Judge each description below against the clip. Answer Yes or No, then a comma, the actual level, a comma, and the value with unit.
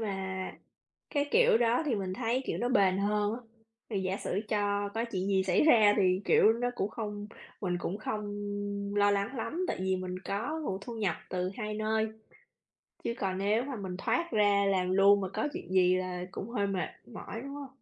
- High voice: Yes, high, 205 Hz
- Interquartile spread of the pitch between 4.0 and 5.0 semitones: No, average, 3.3 semitones